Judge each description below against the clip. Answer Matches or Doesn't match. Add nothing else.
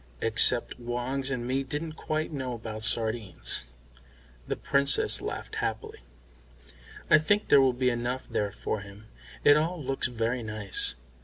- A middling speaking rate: Matches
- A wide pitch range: Doesn't match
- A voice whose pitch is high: Doesn't match